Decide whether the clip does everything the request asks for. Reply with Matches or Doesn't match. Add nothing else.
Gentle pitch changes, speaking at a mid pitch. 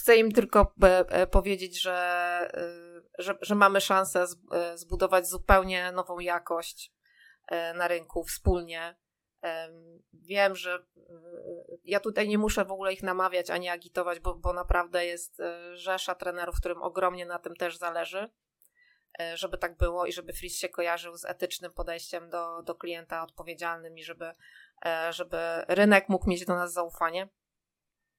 Matches